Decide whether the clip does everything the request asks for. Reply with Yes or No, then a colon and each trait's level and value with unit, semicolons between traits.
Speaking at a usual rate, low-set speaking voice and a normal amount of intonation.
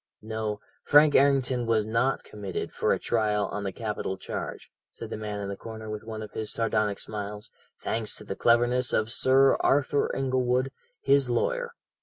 Yes: average, 170 wpm; low, 115 Hz; average, 3.5 semitones